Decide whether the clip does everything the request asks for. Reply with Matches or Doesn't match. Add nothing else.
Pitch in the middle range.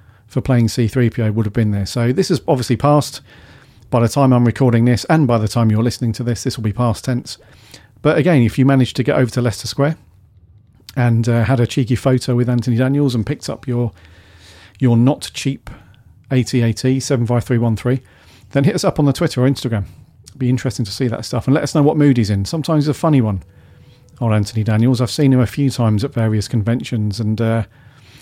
Doesn't match